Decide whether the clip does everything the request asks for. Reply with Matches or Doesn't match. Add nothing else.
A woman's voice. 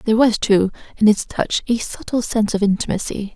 Matches